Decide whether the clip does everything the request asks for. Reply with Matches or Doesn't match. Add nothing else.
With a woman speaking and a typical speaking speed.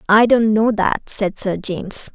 Matches